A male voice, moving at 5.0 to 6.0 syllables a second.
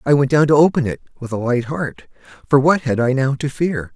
Yes: male; 5.6 syllables/s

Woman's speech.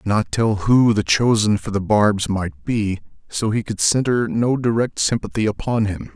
No: male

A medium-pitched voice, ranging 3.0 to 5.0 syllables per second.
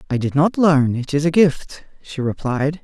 Yes: medium, 150 Hz; 4.5 syllables/s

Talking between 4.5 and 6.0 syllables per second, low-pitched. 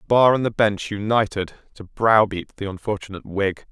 Yes: 5.1 syllables/s; low, 105 Hz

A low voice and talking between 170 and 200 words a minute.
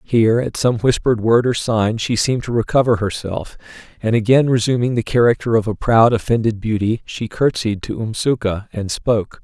Yes: low, 115 Hz; average, 180 wpm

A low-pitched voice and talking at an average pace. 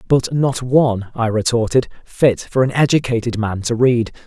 Yes: low, 120 Hz; average, 170 wpm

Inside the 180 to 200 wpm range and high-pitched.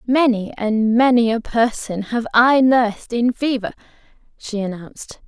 No: slow, 135 wpm; high, 230 Hz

